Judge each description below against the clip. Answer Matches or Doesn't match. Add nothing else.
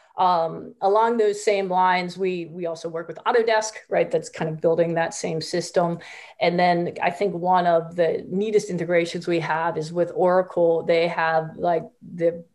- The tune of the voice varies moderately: Doesn't match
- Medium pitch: Matches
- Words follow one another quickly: Doesn't match